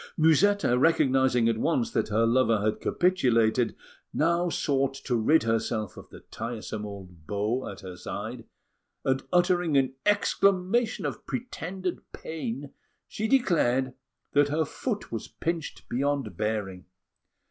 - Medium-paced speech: No, slow, 130 wpm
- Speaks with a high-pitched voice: No, low, 135 Hz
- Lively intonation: Yes, wide, 7.3 semitones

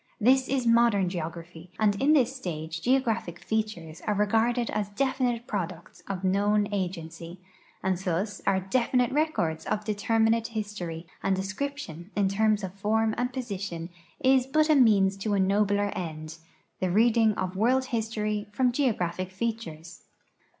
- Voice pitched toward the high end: Yes, high, 210 Hz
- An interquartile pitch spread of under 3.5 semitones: No, average, 4.2 semitones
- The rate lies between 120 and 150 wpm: Yes, average, 145 wpm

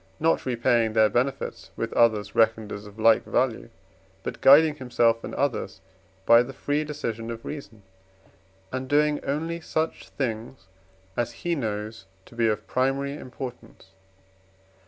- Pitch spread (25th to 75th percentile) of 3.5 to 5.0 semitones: Yes, average, 4.0 semitones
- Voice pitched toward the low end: Yes, low, 120 Hz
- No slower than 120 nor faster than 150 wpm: Yes, average, 140 wpm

